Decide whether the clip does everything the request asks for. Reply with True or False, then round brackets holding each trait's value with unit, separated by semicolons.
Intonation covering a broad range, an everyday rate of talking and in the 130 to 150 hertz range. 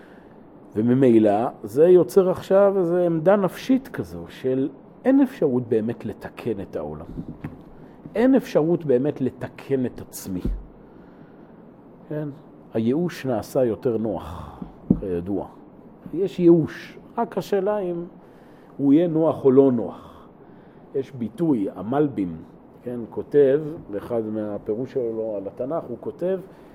True (7.6 semitones; 110 wpm; 140 Hz)